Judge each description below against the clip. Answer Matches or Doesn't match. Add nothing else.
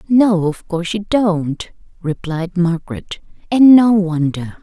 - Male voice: Doesn't match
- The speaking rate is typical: Doesn't match